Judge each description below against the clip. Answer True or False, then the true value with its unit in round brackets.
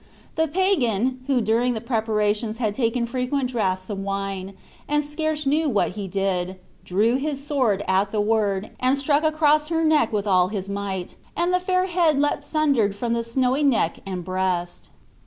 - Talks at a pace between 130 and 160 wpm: False (175 wpm)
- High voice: True (235 Hz)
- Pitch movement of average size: False (6.7 semitones)